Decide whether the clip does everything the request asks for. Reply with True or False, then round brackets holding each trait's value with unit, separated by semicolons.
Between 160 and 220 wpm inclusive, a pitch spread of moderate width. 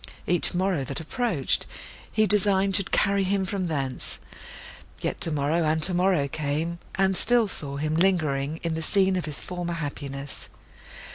False (150 wpm; 4.4 semitones)